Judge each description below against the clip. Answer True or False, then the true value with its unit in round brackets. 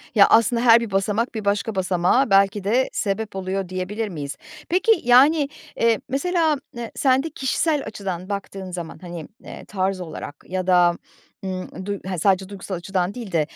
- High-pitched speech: True (200 Hz)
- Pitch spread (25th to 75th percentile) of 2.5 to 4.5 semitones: True (4.0 semitones)